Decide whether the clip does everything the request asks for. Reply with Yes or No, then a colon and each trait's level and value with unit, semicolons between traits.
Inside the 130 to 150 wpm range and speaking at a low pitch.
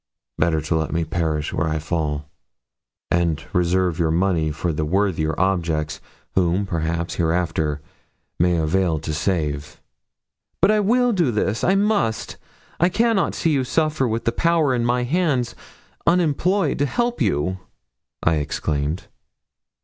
Yes: average, 140 wpm; very low, 90 Hz